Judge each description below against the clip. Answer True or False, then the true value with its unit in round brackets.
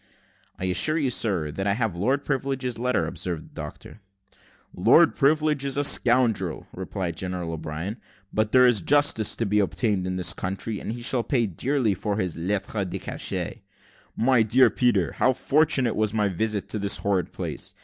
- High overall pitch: False (110 Hz)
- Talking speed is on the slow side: False (180 wpm)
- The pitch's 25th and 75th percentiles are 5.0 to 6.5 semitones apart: True (5.3 semitones)